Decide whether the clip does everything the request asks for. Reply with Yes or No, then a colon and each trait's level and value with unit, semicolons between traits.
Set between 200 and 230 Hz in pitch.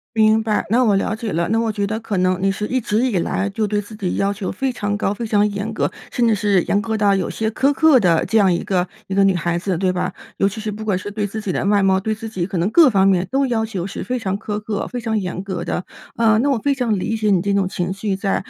Yes: high, 205 Hz